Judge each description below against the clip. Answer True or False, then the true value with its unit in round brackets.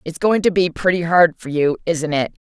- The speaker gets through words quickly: True (245 wpm)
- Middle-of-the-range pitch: True (170 Hz)